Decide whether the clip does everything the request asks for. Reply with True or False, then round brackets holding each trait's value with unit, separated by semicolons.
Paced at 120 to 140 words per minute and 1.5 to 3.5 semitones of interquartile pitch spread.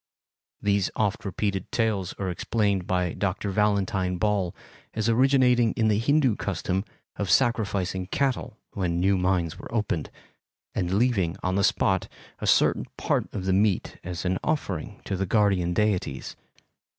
False (150 wpm; 2.9 semitones)